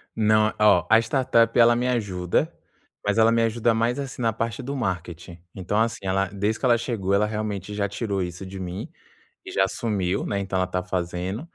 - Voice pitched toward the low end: Yes, low, 105 Hz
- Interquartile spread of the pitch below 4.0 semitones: Yes, average, 3.6 semitones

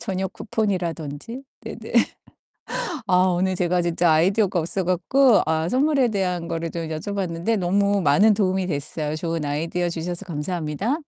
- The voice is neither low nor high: Yes, medium, 180 Hz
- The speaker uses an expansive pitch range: No, average, 3.3 semitones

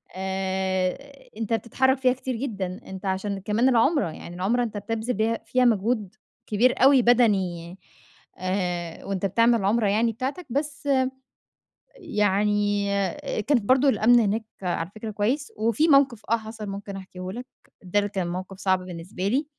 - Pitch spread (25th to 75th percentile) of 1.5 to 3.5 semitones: No, average, 4.1 semitones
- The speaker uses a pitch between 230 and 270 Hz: No, high, 210 Hz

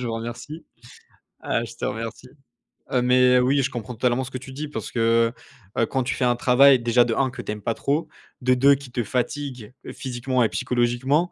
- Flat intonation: Yes, narrow, 1.9 semitones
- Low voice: Yes, low, 125 Hz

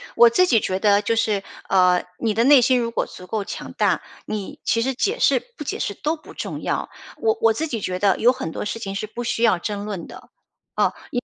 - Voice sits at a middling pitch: No, high, 225 Hz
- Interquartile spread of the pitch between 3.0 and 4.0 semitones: Yes, average, 3.6 semitones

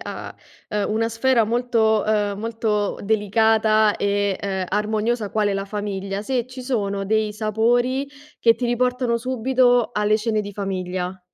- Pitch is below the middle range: No, high, 215 Hz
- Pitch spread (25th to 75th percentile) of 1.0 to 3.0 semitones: Yes, average, 2.7 semitones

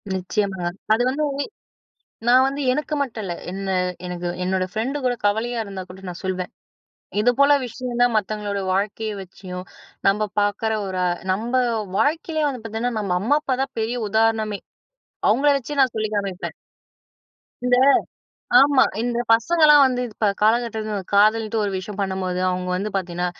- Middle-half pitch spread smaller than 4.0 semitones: No, average, 4.3 semitones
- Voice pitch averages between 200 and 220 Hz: Yes, high, 215 Hz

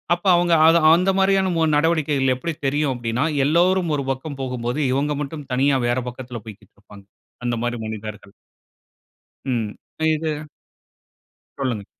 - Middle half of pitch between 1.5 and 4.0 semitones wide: No, average, 5.0 semitones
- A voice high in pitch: No, low, 135 Hz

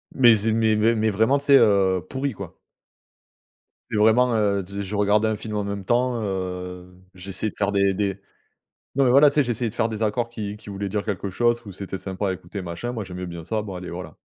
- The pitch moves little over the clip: No, average, 3.0 semitones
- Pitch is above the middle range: No, low, 105 Hz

